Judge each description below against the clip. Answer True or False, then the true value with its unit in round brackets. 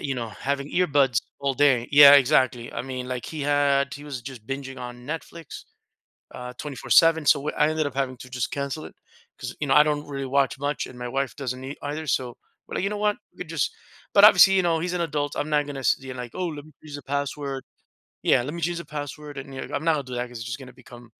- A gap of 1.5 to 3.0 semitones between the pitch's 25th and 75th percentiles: True (2.7 semitones)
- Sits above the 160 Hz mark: False (140 Hz)